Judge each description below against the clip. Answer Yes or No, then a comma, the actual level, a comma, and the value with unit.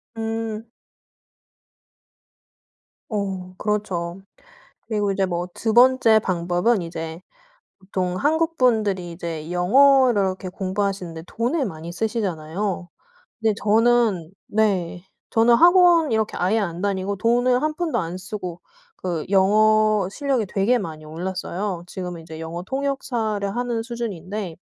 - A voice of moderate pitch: No, high, 200 Hz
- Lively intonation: No, average, 4.3 semitones